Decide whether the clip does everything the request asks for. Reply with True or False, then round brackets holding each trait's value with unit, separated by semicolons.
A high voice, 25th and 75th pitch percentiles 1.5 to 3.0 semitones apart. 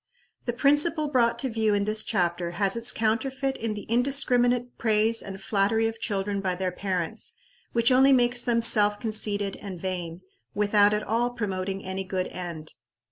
False (215 Hz; 3.8 semitones)